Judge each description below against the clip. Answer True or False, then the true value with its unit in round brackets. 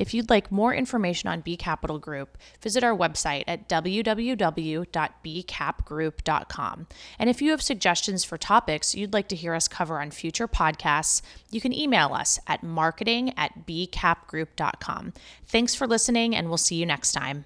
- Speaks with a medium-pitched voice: True (175 Hz)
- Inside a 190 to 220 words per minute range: False (160 wpm)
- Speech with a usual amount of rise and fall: False (6.2 semitones)